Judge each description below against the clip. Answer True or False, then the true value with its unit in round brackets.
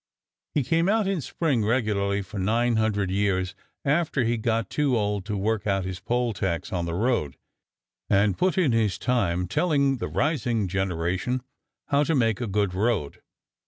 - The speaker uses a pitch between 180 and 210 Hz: False (110 Hz)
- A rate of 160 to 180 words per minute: True (170 wpm)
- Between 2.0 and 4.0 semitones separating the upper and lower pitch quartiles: False (4.8 semitones)